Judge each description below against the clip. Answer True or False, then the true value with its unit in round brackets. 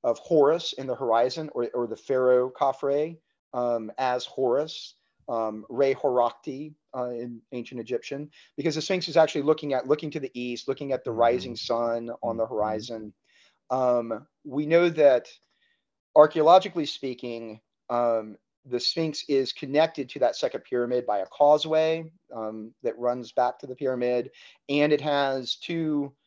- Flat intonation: False (3.9 semitones)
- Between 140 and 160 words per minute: True (155 wpm)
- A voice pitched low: True (130 Hz)